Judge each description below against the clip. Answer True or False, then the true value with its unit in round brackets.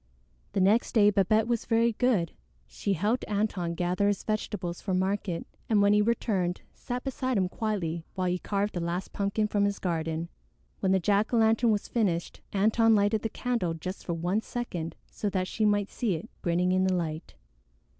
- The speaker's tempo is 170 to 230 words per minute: True (190 wpm)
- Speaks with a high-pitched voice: True (200 Hz)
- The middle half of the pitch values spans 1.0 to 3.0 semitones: False (3.4 semitones)